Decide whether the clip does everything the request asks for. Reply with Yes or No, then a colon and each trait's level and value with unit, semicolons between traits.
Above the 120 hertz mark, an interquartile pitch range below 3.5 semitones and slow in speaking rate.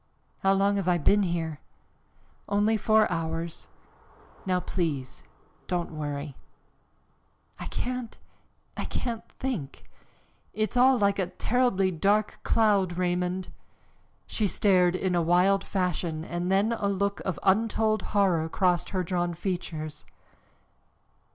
Yes: medium, 185 Hz; average, 3.0 semitones; slow, 120 wpm